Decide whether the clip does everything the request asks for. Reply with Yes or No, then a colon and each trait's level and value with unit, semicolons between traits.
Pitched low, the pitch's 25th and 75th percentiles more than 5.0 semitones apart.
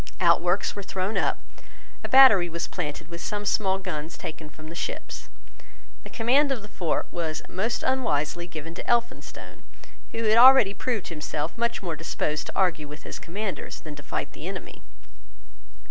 No: medium, 180 Hz; wide, 5.4 semitones